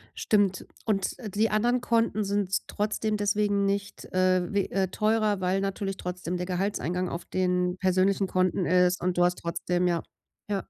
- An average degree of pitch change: No, narrow, 2.2 semitones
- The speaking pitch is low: No, high, 190 Hz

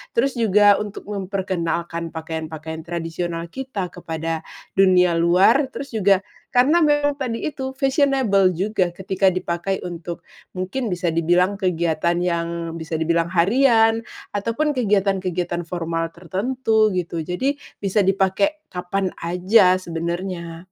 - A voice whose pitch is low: No, medium, 185 Hz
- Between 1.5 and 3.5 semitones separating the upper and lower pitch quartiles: No, average, 4.4 semitones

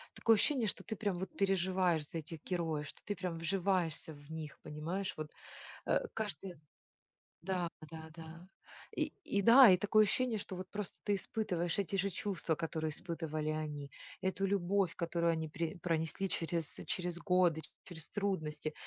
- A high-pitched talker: No, medium, 175 Hz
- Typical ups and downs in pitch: Yes, average, 3.4 semitones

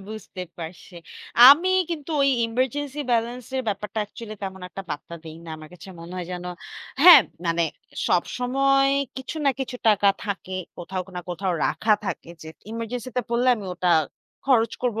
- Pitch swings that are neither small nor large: No, wide, 5.7 semitones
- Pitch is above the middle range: Yes, high, 220 Hz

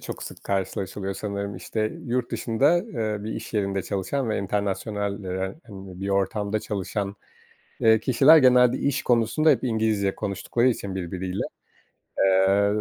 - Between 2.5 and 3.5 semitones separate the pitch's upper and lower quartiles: Yes, average, 3.2 semitones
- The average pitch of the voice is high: No, low, 105 Hz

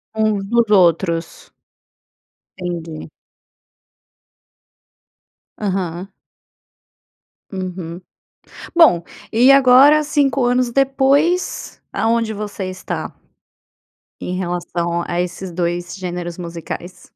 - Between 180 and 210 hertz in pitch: Yes, high, 190 Hz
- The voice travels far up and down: Yes, wide, 5.9 semitones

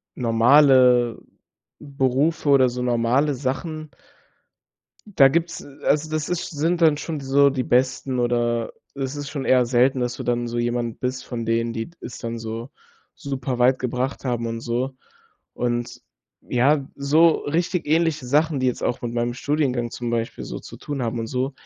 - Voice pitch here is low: Yes, low, 130 Hz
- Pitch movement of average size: Yes, average, 3.2 semitones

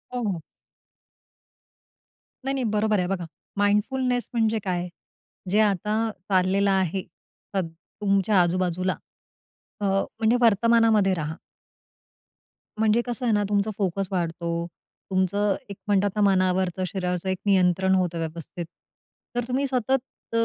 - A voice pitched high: Yes, high, 195 Hz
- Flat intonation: No, average, 3.0 semitones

